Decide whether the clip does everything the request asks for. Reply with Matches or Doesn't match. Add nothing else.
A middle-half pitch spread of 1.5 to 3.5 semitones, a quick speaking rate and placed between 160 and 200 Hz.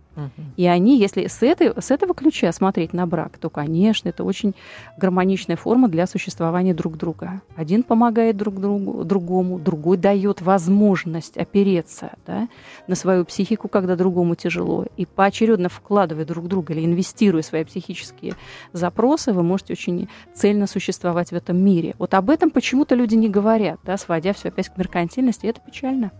Matches